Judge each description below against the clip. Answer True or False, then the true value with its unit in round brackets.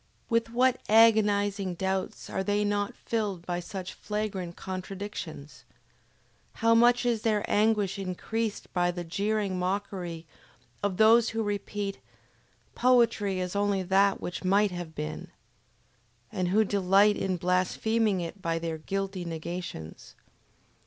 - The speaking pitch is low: False (195 Hz)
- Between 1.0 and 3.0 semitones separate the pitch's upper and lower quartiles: True (2.7 semitones)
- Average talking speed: False (125 wpm)